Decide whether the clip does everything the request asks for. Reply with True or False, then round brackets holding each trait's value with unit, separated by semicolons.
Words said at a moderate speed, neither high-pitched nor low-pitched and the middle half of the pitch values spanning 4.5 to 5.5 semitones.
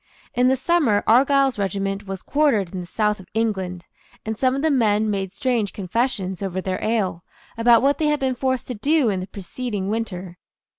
False (195 wpm; 215 Hz; 5.0 semitones)